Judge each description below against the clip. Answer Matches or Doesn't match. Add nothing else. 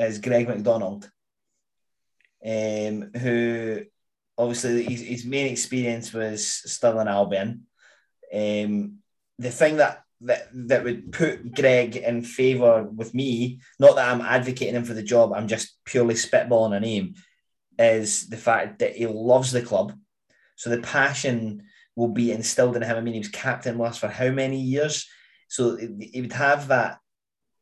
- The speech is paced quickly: Doesn't match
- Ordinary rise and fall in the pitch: Doesn't match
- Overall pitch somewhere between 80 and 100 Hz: Doesn't match